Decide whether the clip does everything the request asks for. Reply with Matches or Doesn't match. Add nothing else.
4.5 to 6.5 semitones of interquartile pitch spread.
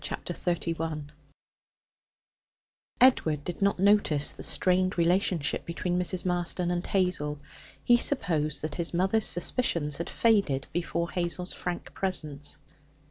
Doesn't match